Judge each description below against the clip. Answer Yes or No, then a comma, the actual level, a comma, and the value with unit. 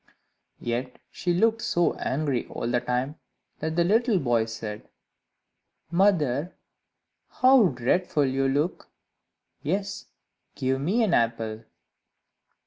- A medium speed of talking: No, slow, 110 wpm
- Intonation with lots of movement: Yes, wide, 6.9 semitones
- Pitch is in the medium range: Yes, medium, 145 Hz